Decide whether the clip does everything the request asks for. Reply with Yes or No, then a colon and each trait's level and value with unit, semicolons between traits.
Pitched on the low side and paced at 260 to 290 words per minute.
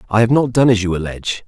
Yes: low, 110 Hz; fast, 285 wpm